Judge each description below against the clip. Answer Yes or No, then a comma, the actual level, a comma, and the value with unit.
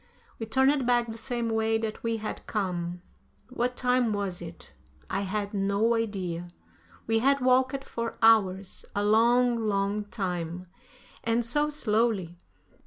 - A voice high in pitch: Yes, high, 220 Hz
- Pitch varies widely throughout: No, average, 3.4 semitones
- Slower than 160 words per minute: Yes, average, 140 wpm